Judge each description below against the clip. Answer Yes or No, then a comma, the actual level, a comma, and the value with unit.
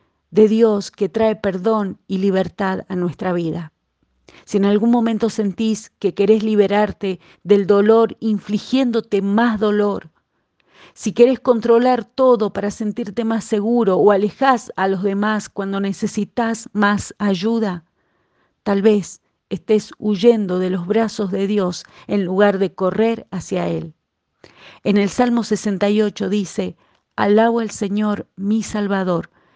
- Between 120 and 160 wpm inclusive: Yes, average, 130 wpm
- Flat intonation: Yes, narrow, 2.1 semitones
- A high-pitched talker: Yes, high, 210 Hz